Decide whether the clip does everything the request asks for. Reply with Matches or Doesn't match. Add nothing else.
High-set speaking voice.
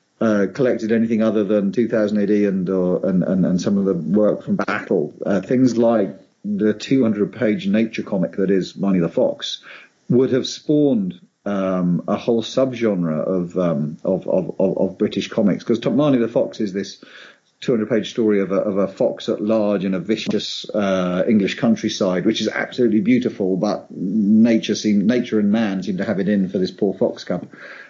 Doesn't match